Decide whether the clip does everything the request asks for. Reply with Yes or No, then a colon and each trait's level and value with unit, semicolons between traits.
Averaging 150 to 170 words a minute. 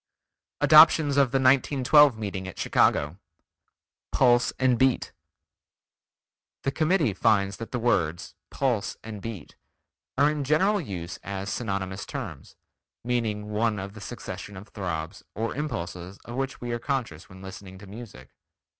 No: average, 140 wpm